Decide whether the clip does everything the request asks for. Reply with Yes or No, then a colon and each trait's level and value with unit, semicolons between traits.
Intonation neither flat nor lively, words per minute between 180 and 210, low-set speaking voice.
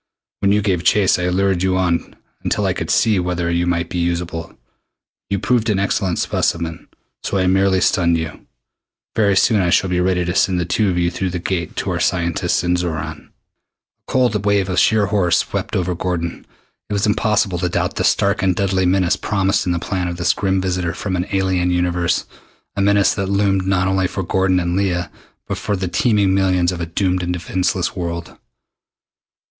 No: narrow, 1.9 semitones; fast, 205 wpm; very low, 90 Hz